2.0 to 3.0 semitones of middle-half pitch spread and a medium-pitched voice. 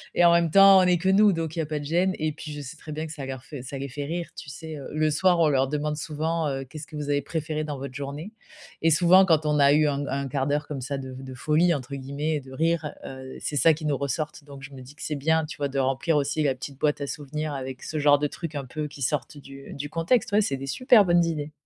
Yes: narrow, 2.6 semitones; medium, 150 Hz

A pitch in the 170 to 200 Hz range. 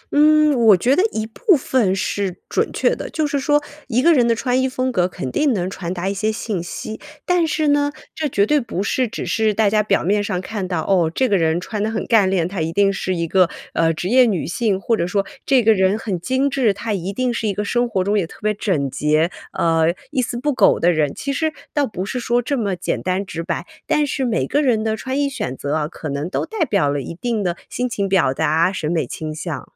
No: high, 210 Hz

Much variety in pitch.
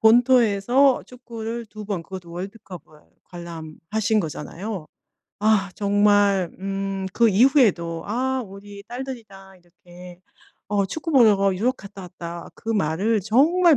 No: average, 3.9 semitones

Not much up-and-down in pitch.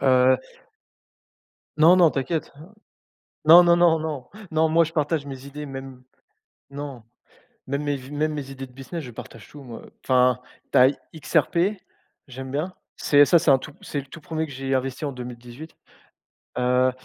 No: average, 3.3 semitones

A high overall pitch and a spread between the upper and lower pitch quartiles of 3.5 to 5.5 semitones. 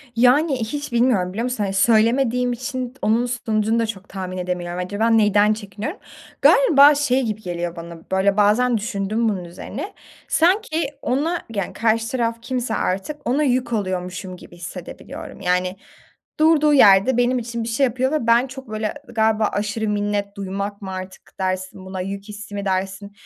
Yes: high, 220 Hz; average, 4.3 semitones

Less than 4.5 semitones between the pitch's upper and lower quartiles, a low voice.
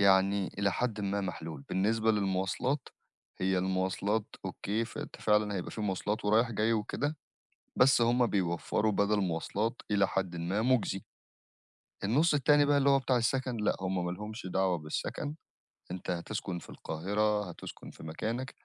Yes: average, 3.5 semitones; low, 105 Hz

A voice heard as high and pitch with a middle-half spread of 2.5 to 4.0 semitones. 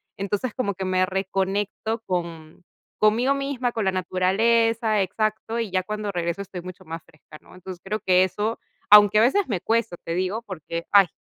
Yes: high, 195 Hz; average, 3.2 semitones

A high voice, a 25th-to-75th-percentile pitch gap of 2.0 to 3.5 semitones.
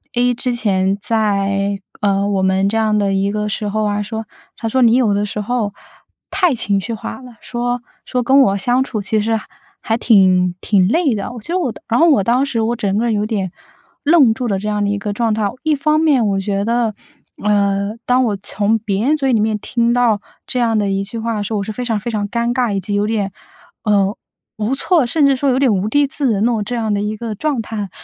Yes: high, 220 Hz; average, 3.1 semitones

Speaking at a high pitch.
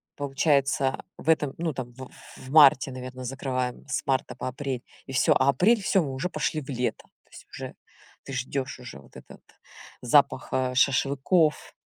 No: low, 135 Hz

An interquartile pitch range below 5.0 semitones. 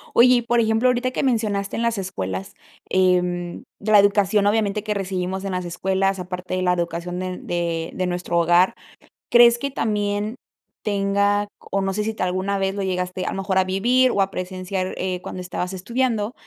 Yes: narrow, 2.6 semitones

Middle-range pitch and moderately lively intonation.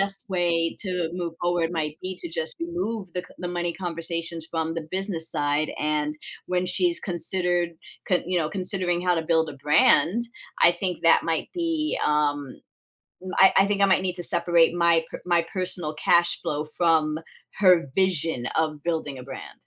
No: medium, 175 Hz; narrow, 2.3 semitones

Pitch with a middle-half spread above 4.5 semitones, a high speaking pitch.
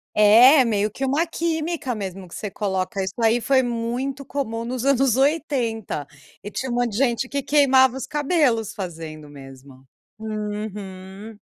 Yes: average, 5.2 semitones; high, 230 Hz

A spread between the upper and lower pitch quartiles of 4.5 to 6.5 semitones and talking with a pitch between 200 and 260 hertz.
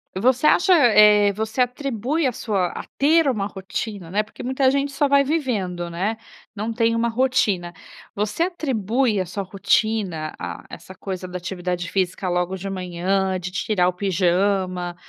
Yes: average, 5.2 semitones; high, 205 Hz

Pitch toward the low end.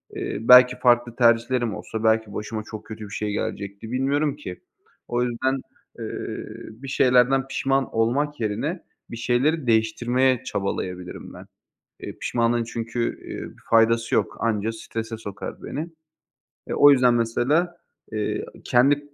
Yes: low, 120 Hz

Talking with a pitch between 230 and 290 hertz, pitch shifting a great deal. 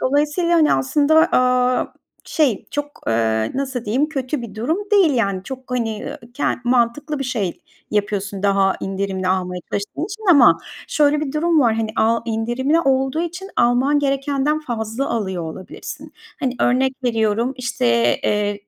Yes: very high, 250 Hz; wide, 5.7 semitones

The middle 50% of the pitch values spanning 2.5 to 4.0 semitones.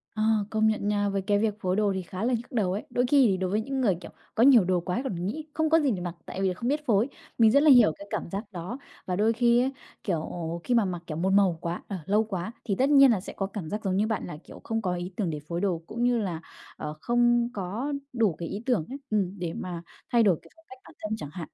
No: average, 4.6 semitones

